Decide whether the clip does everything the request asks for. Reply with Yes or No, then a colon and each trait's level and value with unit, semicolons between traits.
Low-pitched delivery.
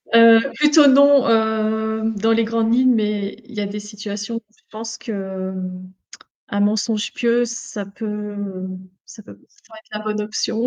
No: high, 220 Hz